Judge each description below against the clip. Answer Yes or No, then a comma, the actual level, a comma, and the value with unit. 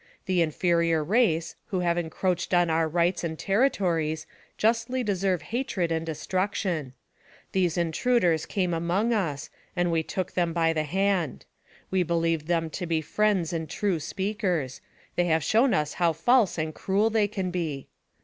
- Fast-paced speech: No, average, 160 wpm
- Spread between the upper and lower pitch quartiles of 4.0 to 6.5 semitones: No, average, 3.3 semitones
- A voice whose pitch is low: No, medium, 175 Hz